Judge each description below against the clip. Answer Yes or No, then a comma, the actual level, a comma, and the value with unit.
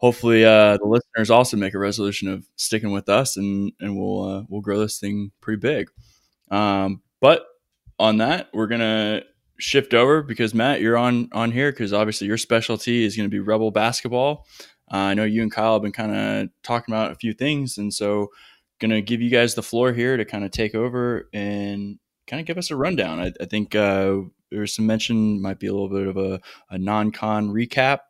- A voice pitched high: No, low, 110 Hz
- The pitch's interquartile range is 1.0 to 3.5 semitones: Yes, narrow, 2.5 semitones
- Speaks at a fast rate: Yes, fast, 210 wpm